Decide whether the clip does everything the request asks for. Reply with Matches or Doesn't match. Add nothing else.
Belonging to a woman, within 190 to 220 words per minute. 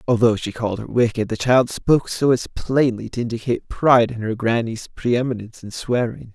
Doesn't match